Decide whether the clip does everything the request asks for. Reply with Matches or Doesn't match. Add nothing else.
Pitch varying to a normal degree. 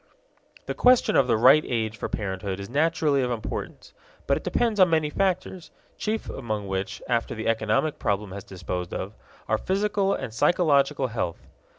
Doesn't match